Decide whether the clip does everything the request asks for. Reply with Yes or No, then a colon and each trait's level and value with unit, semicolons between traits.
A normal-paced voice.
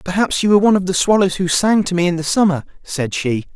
No: fast, 270 wpm